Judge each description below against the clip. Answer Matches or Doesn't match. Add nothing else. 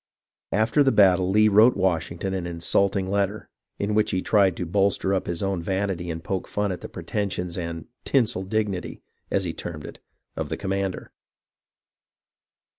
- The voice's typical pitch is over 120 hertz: Doesn't match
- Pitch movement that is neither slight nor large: Doesn't match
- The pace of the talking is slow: Doesn't match